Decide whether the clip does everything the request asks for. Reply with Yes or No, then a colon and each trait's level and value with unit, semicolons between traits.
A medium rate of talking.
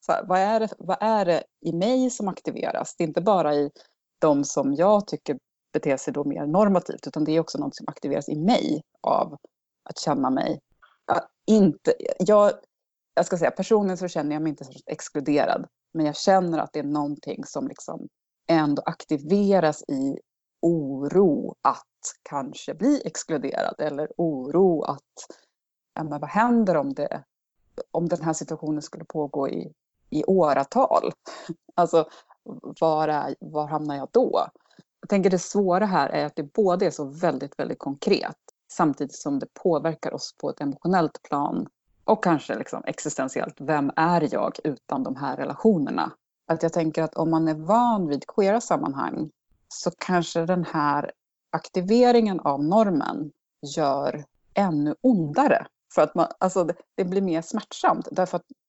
Yes: average, 165 wpm